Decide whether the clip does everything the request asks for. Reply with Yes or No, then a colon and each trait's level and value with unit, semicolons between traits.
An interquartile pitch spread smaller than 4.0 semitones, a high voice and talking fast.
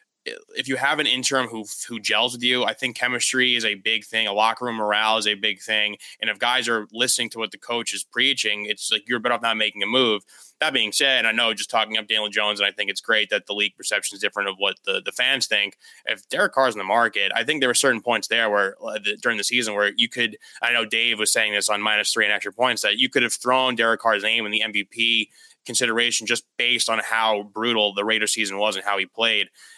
No: narrow, 2.5 semitones; low, 115 Hz; fast, 265 wpm